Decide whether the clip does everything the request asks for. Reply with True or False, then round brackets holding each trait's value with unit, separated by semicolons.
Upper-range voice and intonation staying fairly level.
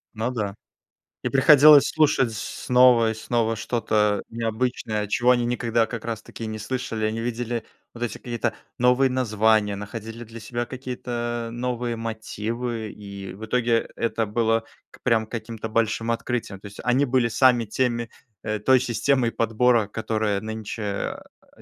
False (115 Hz; 2.0 semitones)